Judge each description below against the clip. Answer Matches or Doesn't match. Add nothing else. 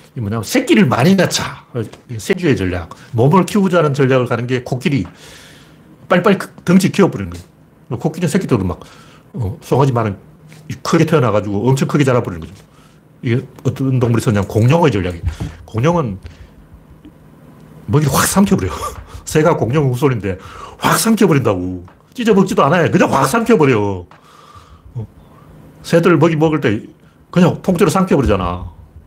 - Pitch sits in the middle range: Doesn't match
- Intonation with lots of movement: Matches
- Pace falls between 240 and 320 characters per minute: Doesn't match